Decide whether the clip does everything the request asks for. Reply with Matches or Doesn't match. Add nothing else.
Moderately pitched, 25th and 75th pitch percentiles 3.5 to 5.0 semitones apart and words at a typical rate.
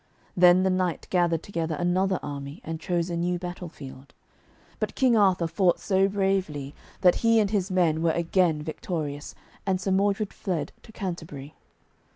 Doesn't match